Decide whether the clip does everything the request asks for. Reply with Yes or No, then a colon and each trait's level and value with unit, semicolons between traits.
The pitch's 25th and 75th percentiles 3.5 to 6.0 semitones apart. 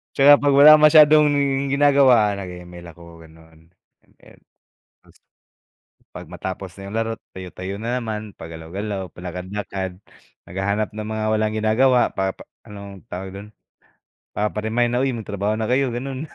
Yes: average, 4.6 semitones